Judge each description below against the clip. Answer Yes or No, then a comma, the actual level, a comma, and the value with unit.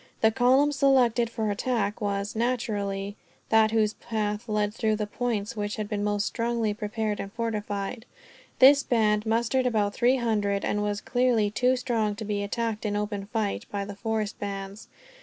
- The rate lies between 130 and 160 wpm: No, average, 170 wpm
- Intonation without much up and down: Yes, narrow, 2.3 semitones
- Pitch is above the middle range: Yes, high, 215 Hz